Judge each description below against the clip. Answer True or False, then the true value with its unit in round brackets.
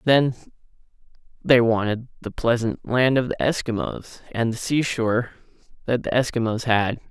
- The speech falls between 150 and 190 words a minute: False (135 wpm)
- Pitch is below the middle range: True (120 Hz)